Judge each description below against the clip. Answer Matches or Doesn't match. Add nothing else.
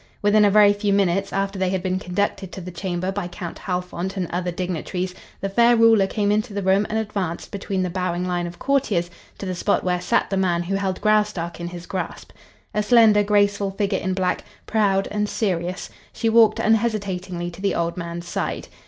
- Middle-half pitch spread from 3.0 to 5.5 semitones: Doesn't match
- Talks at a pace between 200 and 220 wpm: Matches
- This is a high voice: Matches